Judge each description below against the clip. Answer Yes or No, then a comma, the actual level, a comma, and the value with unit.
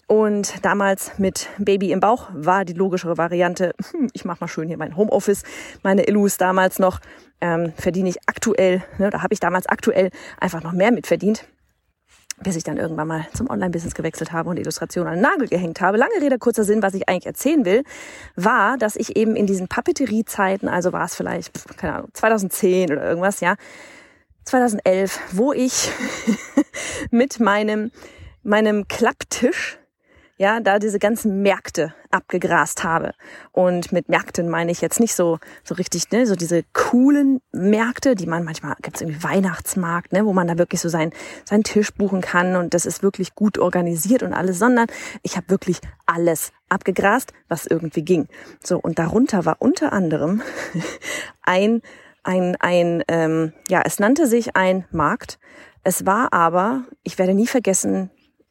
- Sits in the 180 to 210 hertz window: Yes, high, 190 Hz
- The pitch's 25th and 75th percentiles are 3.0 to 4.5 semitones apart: Yes, average, 3.9 semitones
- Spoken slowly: No, average, 175 wpm